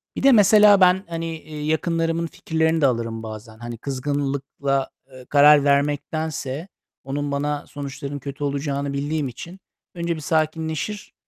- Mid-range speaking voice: Yes, medium, 145 Hz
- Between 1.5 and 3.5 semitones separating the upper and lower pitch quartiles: Yes, average, 2.8 semitones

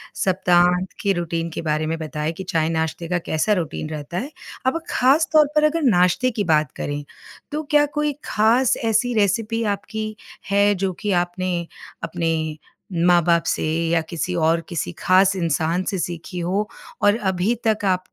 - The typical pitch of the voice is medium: Yes, medium, 180 Hz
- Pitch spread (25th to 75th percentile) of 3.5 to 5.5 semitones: Yes, average, 4.5 semitones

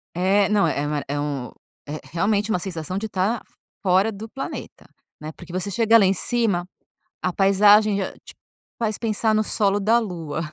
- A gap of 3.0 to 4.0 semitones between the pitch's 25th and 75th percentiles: Yes, average, 3.6 semitones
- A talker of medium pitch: No, high, 195 Hz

